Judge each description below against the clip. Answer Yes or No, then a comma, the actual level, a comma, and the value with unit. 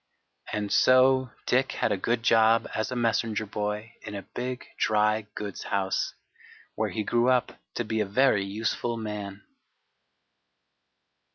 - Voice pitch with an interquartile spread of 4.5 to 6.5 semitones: No, narrow, 2.4 semitones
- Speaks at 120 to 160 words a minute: Yes, average, 145 wpm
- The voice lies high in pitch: No, low, 110 Hz